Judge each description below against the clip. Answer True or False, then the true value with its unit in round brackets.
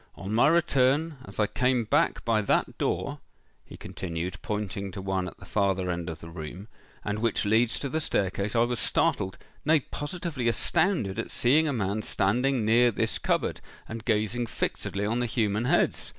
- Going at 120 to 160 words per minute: False (180 wpm)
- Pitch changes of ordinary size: True (4.4 semitones)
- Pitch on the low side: True (110 Hz)